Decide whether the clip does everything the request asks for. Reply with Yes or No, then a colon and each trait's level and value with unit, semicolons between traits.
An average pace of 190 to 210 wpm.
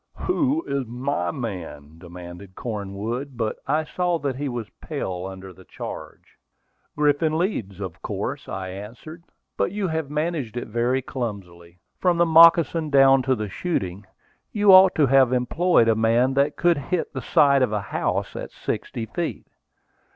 No: average, 160 wpm